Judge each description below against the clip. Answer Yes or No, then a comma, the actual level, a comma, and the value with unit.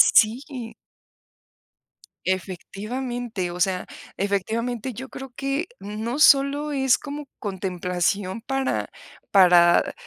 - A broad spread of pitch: Yes, wide, 6.0 semitones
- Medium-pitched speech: No, high, 225 Hz